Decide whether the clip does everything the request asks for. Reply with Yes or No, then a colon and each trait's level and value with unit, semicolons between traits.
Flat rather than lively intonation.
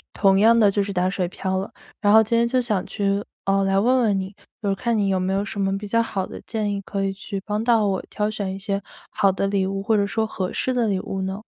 Yes: narrow, 1.9 semitones